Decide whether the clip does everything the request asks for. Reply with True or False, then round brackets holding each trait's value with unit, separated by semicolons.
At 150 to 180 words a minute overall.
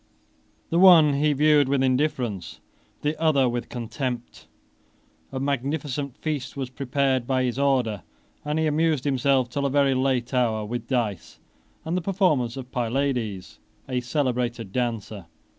False (140 wpm)